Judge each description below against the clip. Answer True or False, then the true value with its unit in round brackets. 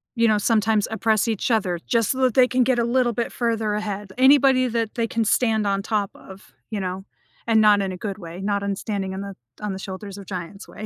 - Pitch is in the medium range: False (215 Hz)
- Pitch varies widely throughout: False (2.8 semitones)